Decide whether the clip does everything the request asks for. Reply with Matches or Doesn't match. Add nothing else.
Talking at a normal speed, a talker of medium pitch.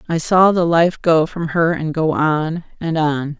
Doesn't match